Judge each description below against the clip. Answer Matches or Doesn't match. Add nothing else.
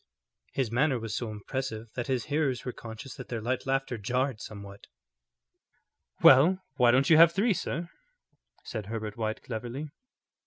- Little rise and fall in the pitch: Doesn't match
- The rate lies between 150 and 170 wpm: Matches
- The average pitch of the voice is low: Matches